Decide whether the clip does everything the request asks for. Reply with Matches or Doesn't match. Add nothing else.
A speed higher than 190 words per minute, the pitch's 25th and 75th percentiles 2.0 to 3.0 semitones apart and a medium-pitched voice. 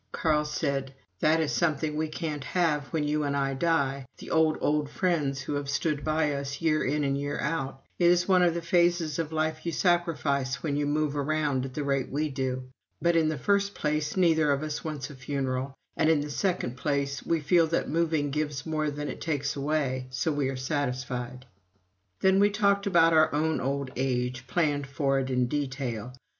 Matches